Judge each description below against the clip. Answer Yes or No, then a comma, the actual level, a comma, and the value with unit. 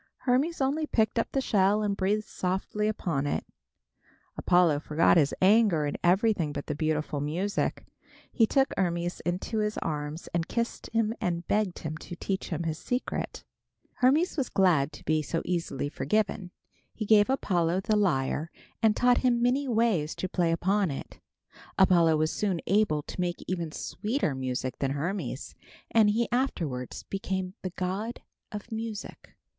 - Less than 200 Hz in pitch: Yes, medium, 185 Hz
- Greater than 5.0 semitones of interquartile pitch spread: Yes, wide, 5.4 semitones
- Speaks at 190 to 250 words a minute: No, average, 160 wpm